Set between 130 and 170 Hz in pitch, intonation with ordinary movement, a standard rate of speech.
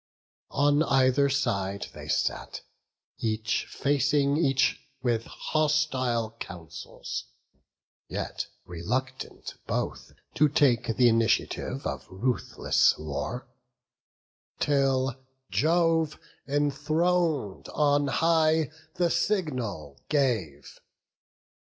No: low, 135 Hz; average, 4.9 semitones; slow, 80 wpm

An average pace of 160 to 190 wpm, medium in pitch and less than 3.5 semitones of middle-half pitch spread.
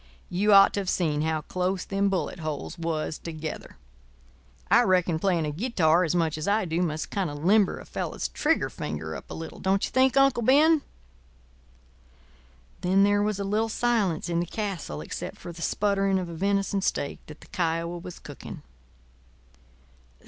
No: average, 180 wpm; medium, 180 Hz; average, 3.8 semitones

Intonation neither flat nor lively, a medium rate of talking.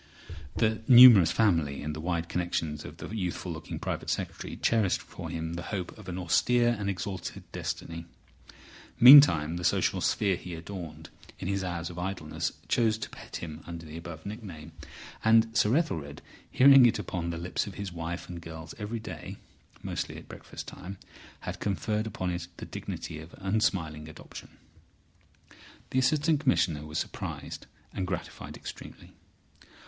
Yes: average, 4.7 semitones; average, 160 wpm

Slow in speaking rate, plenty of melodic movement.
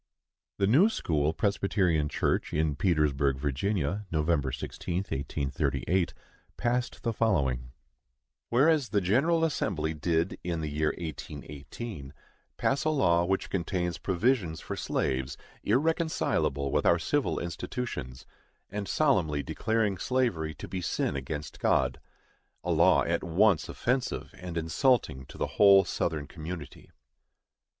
Yes: slow, 125 wpm; wide, 6.5 semitones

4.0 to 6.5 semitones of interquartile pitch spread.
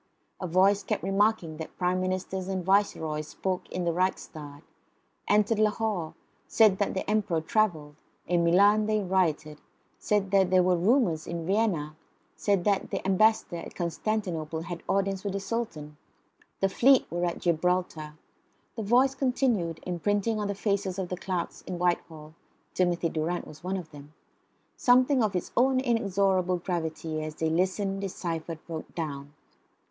No: average, 3.6 semitones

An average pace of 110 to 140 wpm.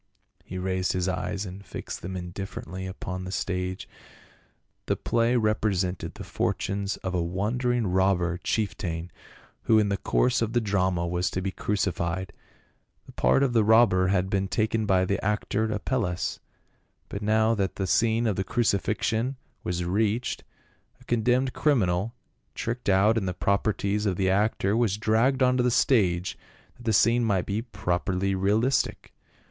No: average, 155 wpm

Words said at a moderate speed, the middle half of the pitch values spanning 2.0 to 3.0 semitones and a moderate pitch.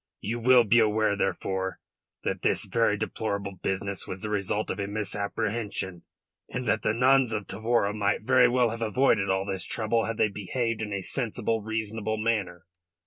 No: average, 175 wpm; narrow, 2.4 semitones; low, 110 Hz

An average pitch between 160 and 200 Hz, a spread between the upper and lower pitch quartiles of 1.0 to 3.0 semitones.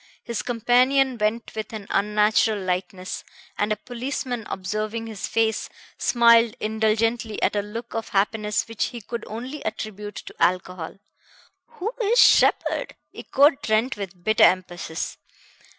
No: high, 220 Hz; narrow, 2.4 semitones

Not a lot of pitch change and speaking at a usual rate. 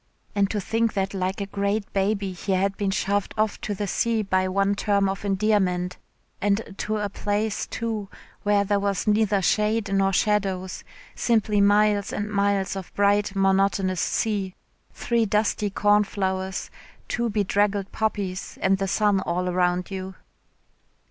Yes: narrow, 1.5 semitones; average, 150 wpm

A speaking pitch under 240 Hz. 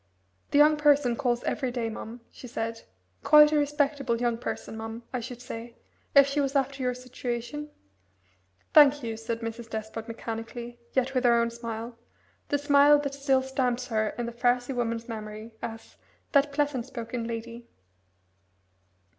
No: high, 245 Hz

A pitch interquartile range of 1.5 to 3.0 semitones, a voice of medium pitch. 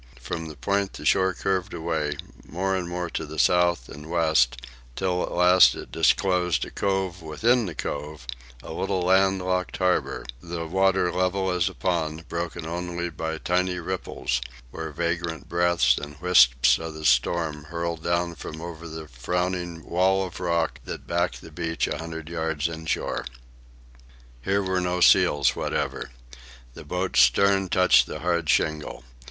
No: narrow, 2.5 semitones; very low, 85 Hz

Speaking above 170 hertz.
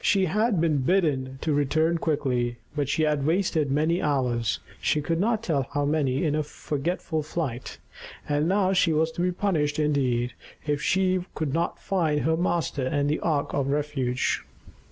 No: medium, 150 Hz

